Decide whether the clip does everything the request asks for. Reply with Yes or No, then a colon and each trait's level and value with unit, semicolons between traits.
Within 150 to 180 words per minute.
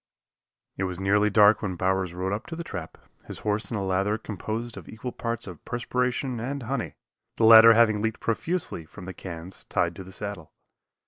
No: average, 195 wpm